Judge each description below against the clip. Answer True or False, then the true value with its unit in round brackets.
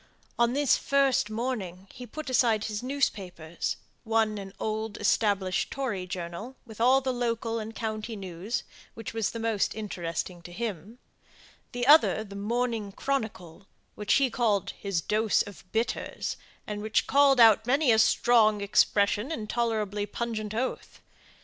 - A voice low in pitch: False (220 Hz)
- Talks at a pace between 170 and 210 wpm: False (150 wpm)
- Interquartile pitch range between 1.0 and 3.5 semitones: True (3.0 semitones)